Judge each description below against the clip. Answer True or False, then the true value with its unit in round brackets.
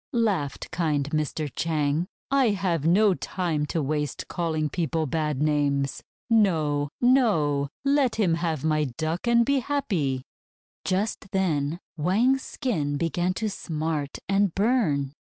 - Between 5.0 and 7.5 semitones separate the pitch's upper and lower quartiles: True (5.5 semitones)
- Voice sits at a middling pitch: True (165 Hz)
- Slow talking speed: True (130 wpm)